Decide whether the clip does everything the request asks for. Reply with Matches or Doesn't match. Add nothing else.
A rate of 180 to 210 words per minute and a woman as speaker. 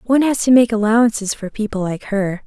Doesn't match